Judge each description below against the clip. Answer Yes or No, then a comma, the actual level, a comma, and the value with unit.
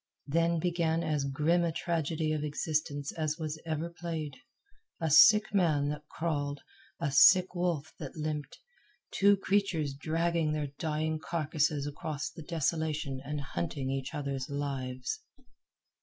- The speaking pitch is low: No, medium, 155 Hz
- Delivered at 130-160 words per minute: Yes, slow, 135 wpm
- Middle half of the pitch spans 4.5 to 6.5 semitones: No, narrow, 2.6 semitones